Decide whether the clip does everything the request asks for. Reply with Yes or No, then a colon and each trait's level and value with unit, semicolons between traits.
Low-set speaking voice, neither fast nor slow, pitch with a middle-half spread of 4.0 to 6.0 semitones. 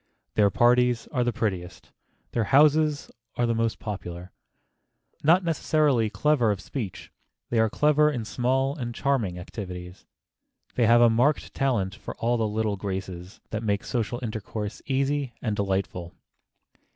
Yes: low, 115 Hz; average, 145 wpm; average, 4.7 semitones